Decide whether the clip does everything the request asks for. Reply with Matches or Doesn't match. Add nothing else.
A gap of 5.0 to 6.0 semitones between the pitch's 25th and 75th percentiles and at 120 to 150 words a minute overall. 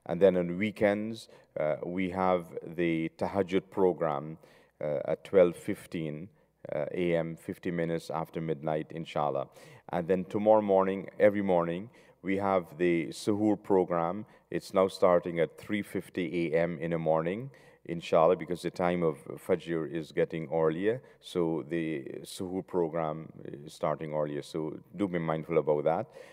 Doesn't match